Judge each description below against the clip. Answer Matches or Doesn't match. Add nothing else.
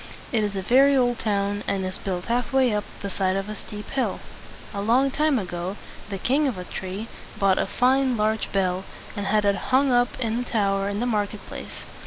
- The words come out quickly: Matches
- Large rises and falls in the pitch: Doesn't match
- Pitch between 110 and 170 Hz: Doesn't match